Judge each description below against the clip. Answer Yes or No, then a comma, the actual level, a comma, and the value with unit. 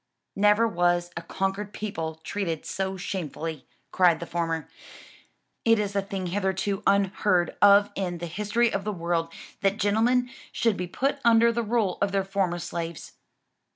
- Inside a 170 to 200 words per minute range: No, average, 155 wpm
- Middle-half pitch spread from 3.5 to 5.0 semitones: No, average, 3.1 semitones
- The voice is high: Yes, high, 195 Hz